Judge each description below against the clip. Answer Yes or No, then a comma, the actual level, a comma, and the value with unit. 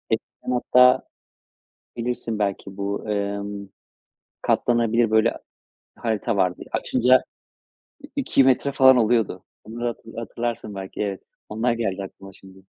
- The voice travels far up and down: No, average, 3.2 semitones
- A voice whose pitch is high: No, low, 110 Hz